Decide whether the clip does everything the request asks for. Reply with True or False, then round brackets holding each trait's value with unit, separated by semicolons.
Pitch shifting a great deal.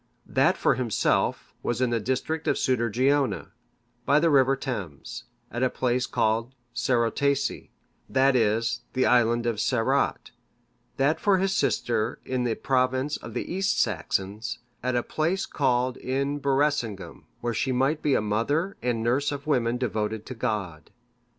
False (3.2 semitones)